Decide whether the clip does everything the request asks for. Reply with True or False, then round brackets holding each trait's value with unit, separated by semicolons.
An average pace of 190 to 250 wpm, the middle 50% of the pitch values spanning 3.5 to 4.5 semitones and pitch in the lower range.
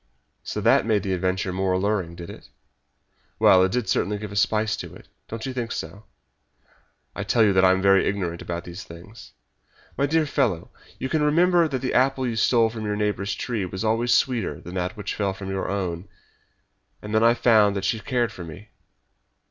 True (205 wpm; 3.9 semitones; 105 Hz)